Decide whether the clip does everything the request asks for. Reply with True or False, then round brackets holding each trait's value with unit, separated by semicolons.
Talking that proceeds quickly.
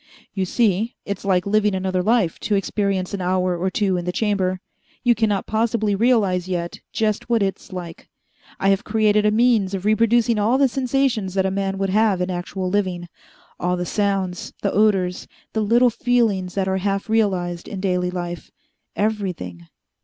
False (175 wpm)